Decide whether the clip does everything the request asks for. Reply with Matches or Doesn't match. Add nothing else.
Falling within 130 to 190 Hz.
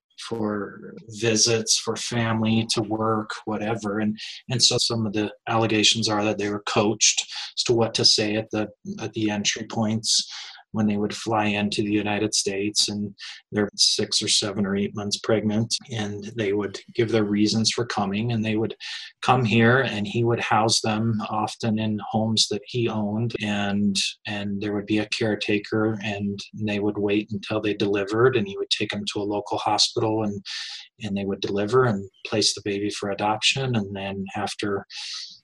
Doesn't match